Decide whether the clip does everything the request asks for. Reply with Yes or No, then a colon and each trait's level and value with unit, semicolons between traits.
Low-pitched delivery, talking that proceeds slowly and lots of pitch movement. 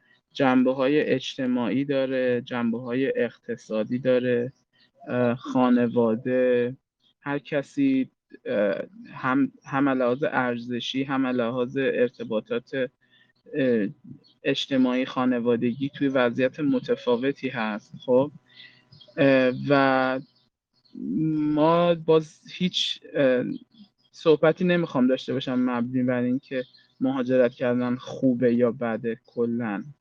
No: low, 130 Hz; slow, 85 wpm; average, 4.1 semitones